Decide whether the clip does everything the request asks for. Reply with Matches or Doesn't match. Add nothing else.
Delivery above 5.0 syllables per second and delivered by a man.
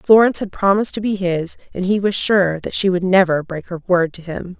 Doesn't match